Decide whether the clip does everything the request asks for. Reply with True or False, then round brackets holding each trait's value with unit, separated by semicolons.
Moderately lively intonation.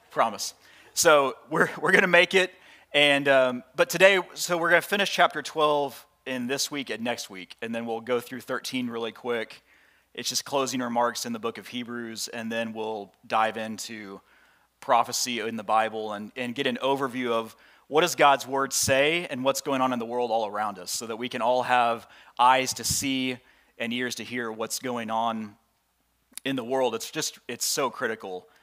True (3.4 semitones)